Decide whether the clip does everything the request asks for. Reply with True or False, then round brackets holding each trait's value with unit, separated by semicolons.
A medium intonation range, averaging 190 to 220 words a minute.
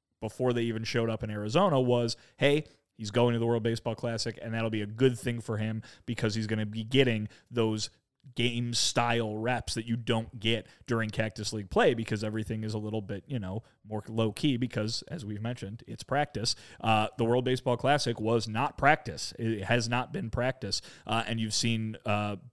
False (1.8 semitones; 205 wpm)